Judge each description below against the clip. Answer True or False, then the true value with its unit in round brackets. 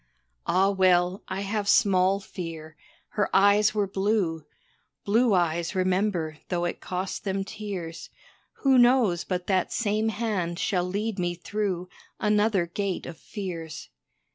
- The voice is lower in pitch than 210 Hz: True (190 Hz)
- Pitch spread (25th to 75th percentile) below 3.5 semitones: True (2.9 semitones)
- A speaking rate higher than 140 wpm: False (135 wpm)